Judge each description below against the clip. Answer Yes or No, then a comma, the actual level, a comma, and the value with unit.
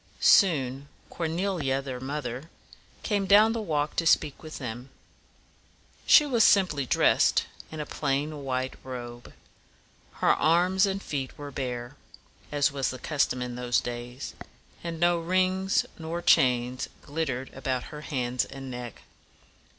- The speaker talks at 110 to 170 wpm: Yes, average, 145 wpm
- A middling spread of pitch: Yes, average, 4.8 semitones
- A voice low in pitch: No, medium, 145 Hz